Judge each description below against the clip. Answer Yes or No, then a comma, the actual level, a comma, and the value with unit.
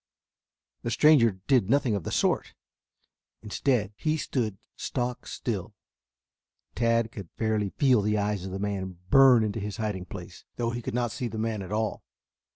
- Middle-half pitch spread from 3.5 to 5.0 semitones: No, average, 3.0 semitones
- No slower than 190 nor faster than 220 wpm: No, average, 165 wpm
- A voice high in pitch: No, low, 110 Hz